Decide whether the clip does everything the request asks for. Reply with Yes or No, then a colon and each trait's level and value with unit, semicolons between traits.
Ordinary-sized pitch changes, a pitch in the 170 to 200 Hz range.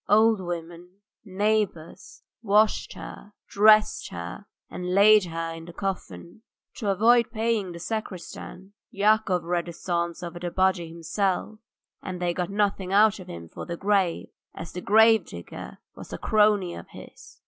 Yes: average, 3.6 semitones; high, 190 Hz